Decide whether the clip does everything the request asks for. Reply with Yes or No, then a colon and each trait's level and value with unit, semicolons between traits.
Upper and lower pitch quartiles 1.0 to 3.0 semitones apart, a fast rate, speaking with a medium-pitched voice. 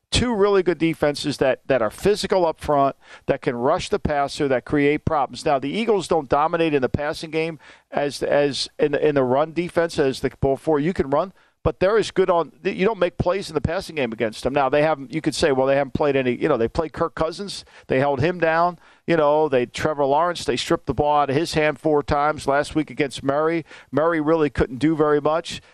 Yes: average, 2.7 semitones; fast, 240 wpm; medium, 155 Hz